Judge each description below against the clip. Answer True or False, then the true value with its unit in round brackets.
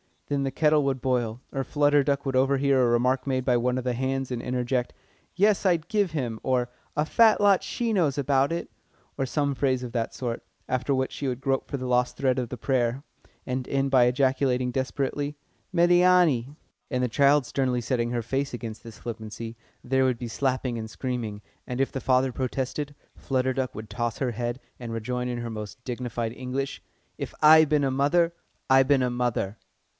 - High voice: False (130 Hz)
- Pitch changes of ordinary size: False (2.2 semitones)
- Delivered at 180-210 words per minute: True (195 wpm)